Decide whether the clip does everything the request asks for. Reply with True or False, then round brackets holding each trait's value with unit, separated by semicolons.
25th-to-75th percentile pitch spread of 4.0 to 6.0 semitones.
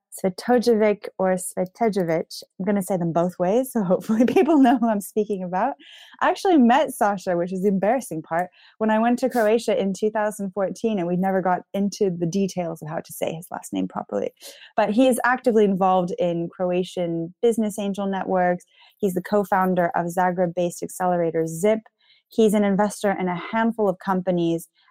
False (3.4 semitones)